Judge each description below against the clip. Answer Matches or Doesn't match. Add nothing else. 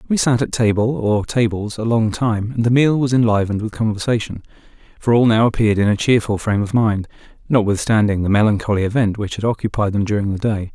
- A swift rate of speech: Doesn't match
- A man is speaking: Matches